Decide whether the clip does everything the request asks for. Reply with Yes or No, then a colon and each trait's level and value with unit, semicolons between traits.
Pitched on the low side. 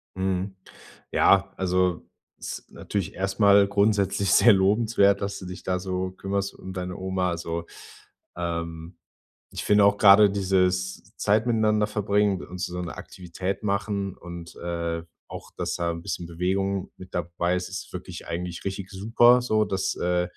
Yes: very low, 95 Hz